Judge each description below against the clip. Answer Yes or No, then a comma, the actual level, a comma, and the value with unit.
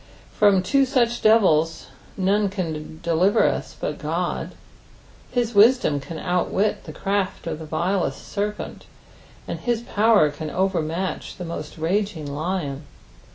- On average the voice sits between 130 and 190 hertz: Yes, medium, 185 Hz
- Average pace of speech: No, slow, 130 wpm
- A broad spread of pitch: No, average, 4.7 semitones